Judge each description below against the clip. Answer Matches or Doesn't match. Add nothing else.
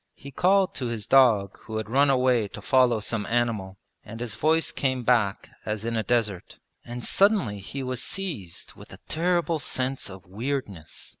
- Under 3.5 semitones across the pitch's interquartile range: Doesn't match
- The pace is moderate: Matches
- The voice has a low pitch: Matches